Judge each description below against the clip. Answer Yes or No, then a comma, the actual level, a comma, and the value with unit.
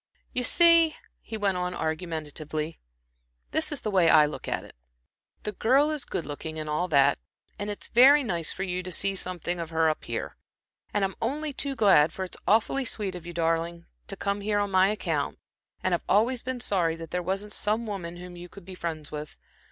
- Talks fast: Yes, fast, 210 wpm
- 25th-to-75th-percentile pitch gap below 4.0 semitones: No, average, 4.5 semitones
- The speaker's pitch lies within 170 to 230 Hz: Yes, medium, 185 Hz